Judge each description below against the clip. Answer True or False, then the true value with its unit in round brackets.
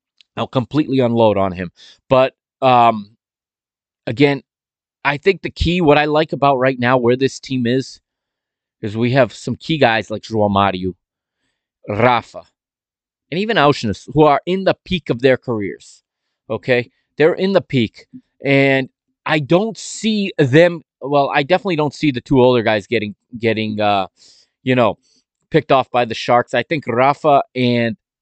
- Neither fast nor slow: True (160 wpm)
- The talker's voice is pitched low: True (130 Hz)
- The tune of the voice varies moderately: True (4.7 semitones)